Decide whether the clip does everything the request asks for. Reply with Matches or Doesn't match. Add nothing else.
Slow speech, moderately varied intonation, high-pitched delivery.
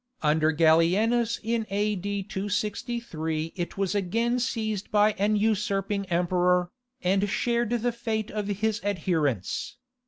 Matches